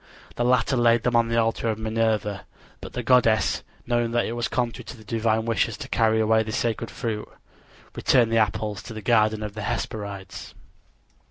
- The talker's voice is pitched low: Yes, low, 110 Hz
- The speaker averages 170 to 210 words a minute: Yes, average, 190 wpm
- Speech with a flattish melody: Yes, narrow, 1.4 semitones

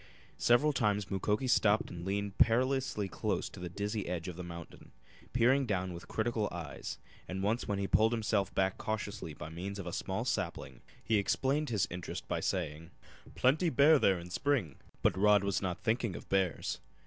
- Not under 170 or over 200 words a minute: Yes, average, 185 wpm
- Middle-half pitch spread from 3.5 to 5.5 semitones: Yes, average, 4.3 semitones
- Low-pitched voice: Yes, low, 100 Hz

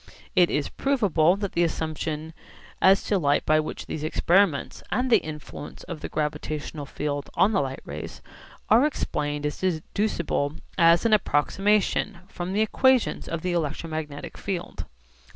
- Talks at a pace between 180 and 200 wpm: No, average, 150 wpm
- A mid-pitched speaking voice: Yes, medium, 165 Hz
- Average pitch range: Yes, average, 4.6 semitones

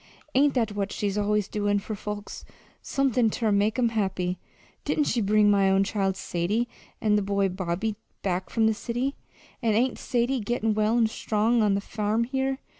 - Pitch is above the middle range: Yes, high, 210 Hz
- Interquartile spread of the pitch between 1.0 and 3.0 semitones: Yes, narrow, 2.6 semitones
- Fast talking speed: No, average, 185 wpm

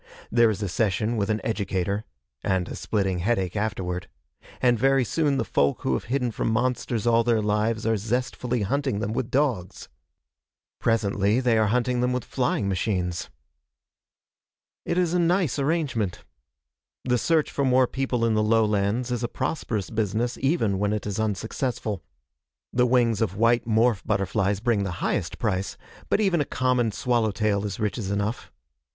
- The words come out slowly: No, average, 165 wpm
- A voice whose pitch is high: No, low, 115 Hz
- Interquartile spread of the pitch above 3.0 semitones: Yes, average, 3.6 semitones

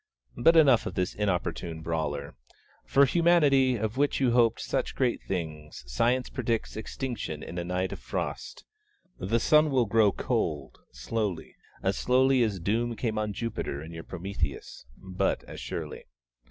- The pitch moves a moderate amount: No, wide, 6.7 semitones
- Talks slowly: No, average, 155 wpm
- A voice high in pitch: No, low, 110 Hz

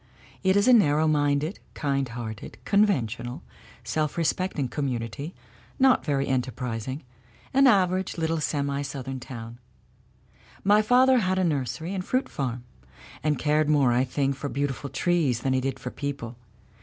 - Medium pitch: Yes, medium, 145 Hz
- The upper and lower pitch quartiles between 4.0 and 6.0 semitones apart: Yes, average, 5.2 semitones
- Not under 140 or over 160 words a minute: Yes, average, 150 wpm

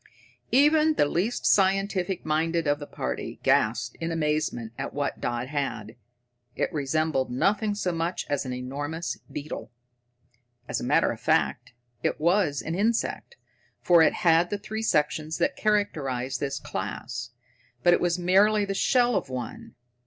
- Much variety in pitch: Yes, wide, 6.2 semitones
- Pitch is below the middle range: No, medium, 160 Hz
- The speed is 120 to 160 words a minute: Yes, average, 150 wpm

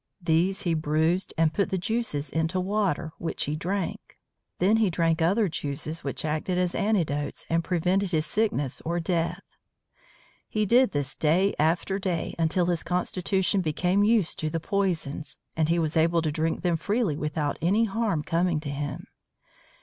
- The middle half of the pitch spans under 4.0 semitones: Yes, average, 3.4 semitones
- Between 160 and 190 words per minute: Yes, average, 165 wpm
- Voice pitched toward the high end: No, medium, 170 Hz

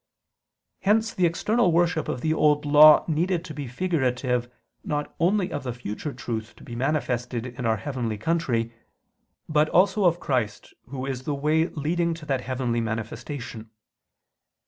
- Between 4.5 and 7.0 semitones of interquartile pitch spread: Yes, average, 5.2 semitones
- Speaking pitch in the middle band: Yes, medium, 145 Hz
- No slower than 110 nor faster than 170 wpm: Yes, average, 155 wpm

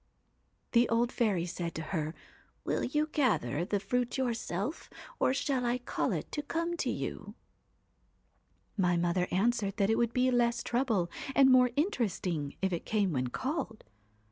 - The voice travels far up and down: Yes, wide, 6.1 semitones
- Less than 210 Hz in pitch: No, high, 230 Hz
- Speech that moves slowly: No, average, 170 wpm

